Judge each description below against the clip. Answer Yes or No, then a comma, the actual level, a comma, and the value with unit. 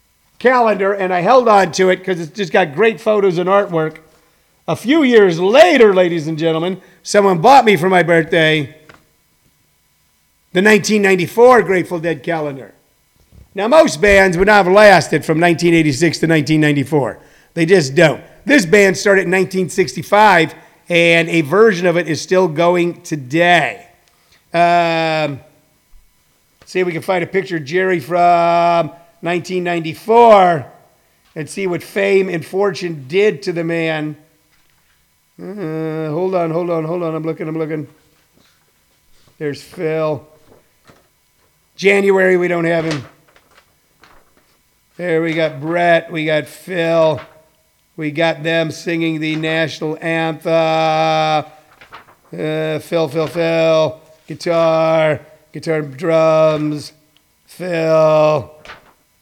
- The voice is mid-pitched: Yes, medium, 165 Hz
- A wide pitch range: No, average, 2.9 semitones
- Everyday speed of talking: No, slow, 125 wpm